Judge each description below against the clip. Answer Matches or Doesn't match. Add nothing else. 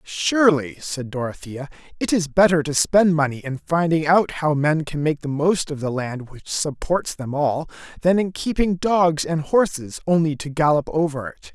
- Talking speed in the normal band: Matches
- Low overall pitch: Doesn't match